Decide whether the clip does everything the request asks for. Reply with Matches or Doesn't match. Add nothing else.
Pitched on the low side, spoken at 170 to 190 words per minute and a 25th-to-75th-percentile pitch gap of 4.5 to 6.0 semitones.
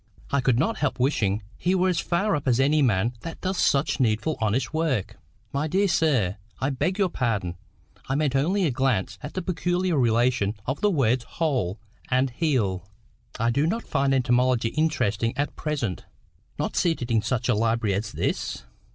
Matches